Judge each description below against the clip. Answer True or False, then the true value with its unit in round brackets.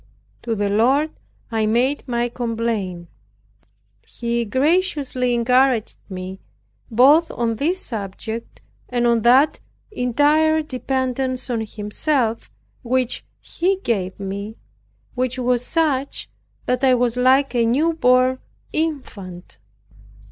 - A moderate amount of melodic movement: True (3.1 semitones)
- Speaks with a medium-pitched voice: False (250 Hz)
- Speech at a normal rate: False (110 wpm)